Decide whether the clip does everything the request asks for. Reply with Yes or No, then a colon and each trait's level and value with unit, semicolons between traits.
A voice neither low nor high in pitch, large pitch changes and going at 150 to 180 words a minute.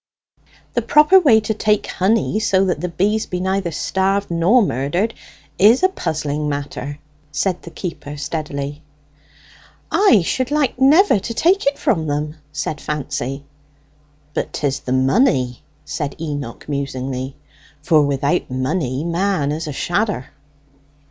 No: medium, 165 Hz; wide, 6.7 semitones; slow, 135 wpm